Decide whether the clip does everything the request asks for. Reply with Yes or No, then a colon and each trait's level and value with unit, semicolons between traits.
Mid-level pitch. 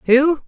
No: very high, 280 Hz